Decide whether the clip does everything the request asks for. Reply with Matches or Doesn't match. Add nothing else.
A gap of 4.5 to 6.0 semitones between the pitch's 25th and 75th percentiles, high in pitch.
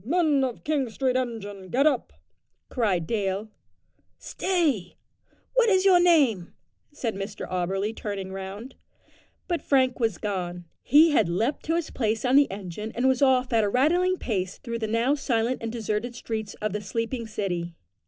Matches